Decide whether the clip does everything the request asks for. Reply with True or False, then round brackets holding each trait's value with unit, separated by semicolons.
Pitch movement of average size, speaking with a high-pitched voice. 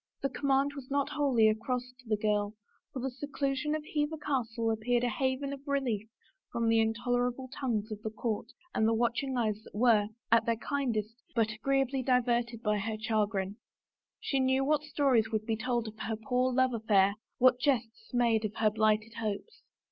True (3.4 semitones; 235 Hz)